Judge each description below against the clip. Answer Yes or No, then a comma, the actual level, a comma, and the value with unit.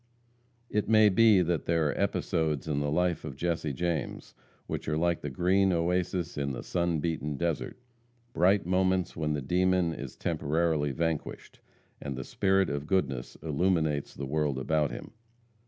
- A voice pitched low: Yes, very low, 80 Hz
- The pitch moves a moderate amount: Yes, average, 3.6 semitones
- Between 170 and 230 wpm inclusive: No, average, 160 wpm